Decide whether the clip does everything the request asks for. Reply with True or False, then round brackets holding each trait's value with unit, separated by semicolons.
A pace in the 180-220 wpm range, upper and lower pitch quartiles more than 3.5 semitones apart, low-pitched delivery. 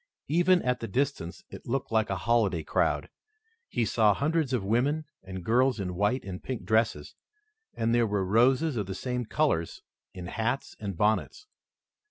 False (170 wpm; 5.0 semitones; 115 Hz)